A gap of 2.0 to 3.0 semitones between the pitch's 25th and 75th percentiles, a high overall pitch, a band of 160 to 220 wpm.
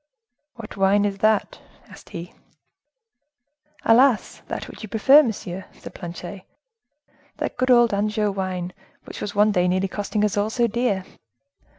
No: average, 2.7 semitones; high, 205 Hz; average, 150 wpm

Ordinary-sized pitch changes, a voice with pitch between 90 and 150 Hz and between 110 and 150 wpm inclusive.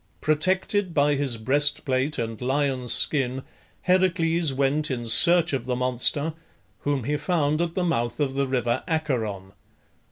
Yes: average, 4.0 semitones; medium, 140 Hz; average, 140 wpm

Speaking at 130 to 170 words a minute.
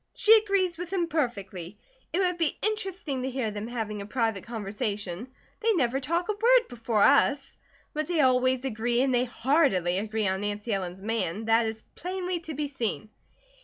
No: average, 180 wpm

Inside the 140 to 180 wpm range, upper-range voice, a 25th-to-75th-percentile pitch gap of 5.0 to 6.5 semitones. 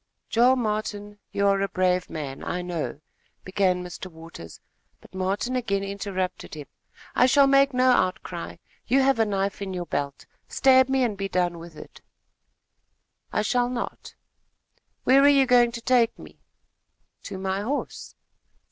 Yes: average, 165 wpm; high, 200 Hz; wide, 5.4 semitones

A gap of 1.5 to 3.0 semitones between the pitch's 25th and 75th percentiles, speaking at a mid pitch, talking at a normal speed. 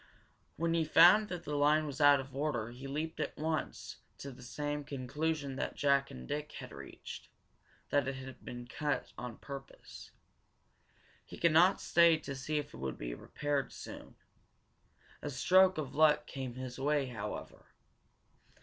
Yes: average, 2.7 semitones; medium, 145 Hz; average, 165 wpm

